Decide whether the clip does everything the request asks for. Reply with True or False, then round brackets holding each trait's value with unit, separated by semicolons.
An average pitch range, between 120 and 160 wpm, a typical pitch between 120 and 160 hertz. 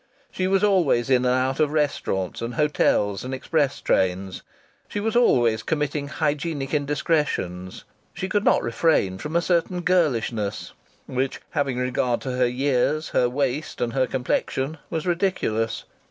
True (4.7 semitones; 150 wpm; 135 Hz)